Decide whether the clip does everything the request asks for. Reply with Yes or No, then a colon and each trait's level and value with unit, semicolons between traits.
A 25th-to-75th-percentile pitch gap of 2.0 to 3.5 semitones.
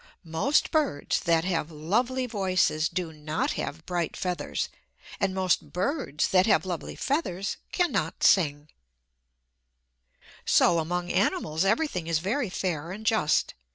No: average, 5.0 semitones